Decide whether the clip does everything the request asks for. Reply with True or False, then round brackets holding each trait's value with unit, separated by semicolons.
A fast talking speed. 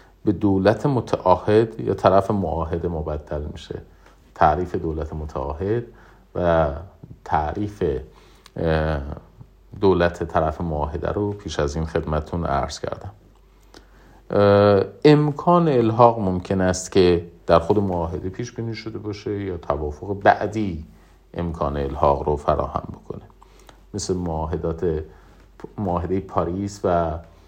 False (105 wpm)